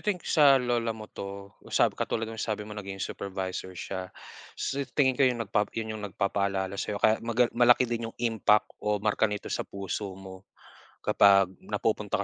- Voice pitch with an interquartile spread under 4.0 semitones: Yes, average, 3.0 semitones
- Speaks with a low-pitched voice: Yes, low, 105 Hz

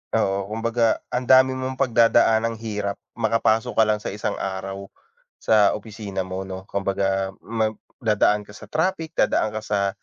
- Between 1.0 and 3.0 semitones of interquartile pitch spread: Yes, average, 2.7 semitones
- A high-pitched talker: No, low, 110 Hz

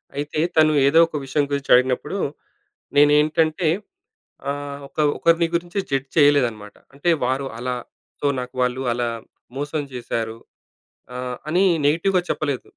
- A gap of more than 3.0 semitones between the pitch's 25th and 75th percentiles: Yes, average, 3.5 semitones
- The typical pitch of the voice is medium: Yes, medium, 145 Hz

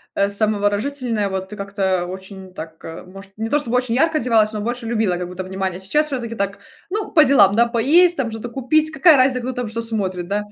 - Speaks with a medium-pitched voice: No, high, 220 Hz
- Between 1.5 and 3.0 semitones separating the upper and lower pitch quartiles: No, average, 4.8 semitones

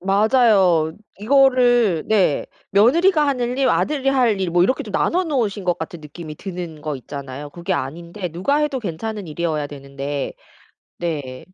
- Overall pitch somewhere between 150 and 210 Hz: Yes, medium, 185 Hz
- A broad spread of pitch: Yes, wide, 7.7 semitones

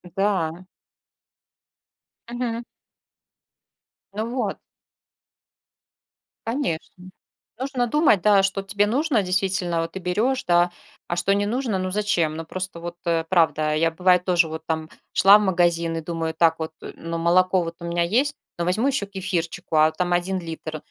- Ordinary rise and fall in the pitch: Yes, average, 3.5 semitones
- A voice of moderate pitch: Yes, medium, 180 Hz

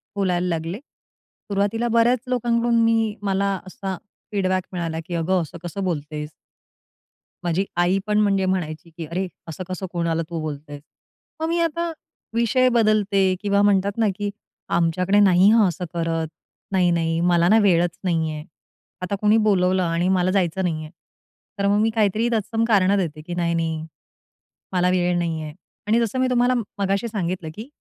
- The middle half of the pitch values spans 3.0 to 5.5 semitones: Yes, average, 3.7 semitones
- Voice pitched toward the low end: No, medium, 185 Hz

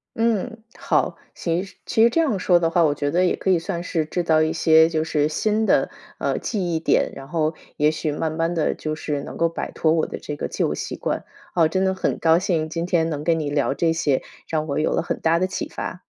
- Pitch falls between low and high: Yes, medium, 165 Hz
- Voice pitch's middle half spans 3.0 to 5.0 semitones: No, narrow, 2.5 semitones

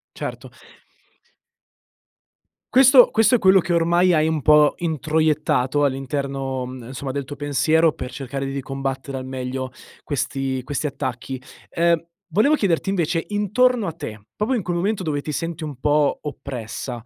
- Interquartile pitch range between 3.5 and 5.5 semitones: Yes, average, 4.3 semitones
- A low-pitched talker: No, medium, 150 Hz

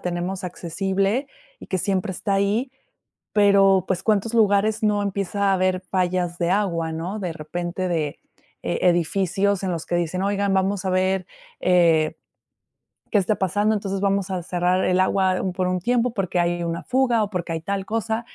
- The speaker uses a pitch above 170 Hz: Yes, high, 190 Hz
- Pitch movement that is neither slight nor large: No, narrow, 2.3 semitones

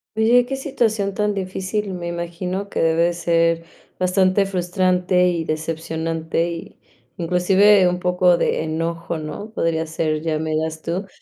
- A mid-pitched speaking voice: Yes, medium, 175 Hz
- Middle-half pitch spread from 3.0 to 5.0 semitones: No, narrow, 2.6 semitones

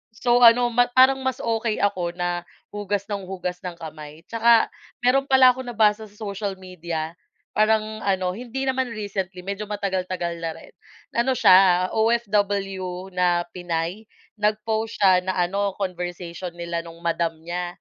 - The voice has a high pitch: Yes, high, 195 Hz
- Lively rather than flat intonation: No, average, 3.8 semitones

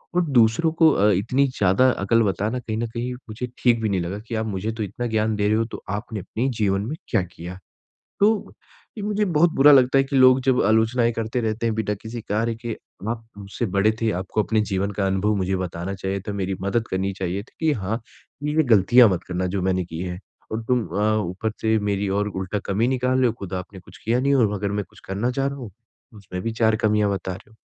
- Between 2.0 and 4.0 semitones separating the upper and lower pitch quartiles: Yes, average, 3.7 semitones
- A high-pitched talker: No, low, 110 Hz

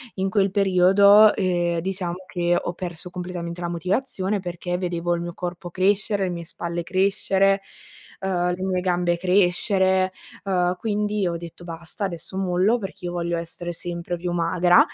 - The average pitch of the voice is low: No, medium, 180 Hz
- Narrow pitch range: Yes, narrow, 1.8 semitones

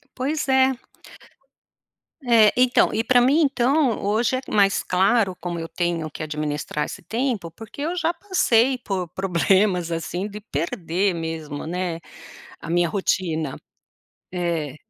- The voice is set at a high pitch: Yes, high, 195 Hz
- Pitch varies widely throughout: Yes, wide, 6.7 semitones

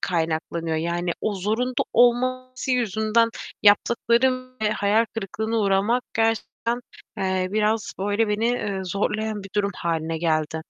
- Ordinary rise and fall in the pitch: Yes, average, 3.8 semitones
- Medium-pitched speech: No, high, 210 Hz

